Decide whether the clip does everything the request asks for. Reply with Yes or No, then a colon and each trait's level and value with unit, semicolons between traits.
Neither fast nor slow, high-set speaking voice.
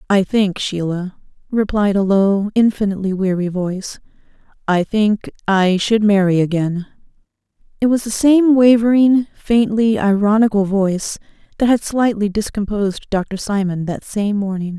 No: slow, 130 wpm; high, 205 Hz